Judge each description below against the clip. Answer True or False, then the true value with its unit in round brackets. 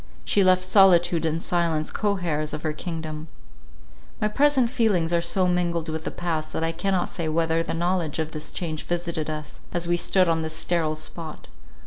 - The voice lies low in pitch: False (170 Hz)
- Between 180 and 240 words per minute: True (190 wpm)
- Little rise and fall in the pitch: True (2.2 semitones)